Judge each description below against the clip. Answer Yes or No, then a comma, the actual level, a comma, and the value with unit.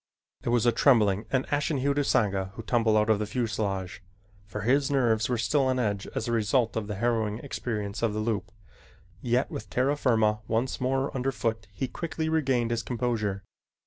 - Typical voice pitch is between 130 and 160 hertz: No, low, 115 Hz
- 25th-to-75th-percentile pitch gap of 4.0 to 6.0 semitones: No, average, 3.4 semitones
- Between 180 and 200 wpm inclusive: Yes, average, 190 wpm